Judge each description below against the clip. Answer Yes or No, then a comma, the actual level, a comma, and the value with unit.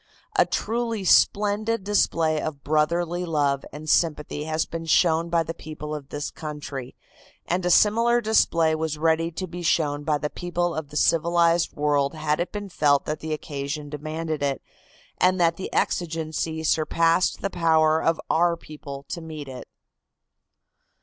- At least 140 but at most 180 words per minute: Yes, average, 160 wpm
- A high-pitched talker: No, medium, 160 Hz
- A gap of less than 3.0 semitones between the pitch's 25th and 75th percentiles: Yes, narrow, 2.5 semitones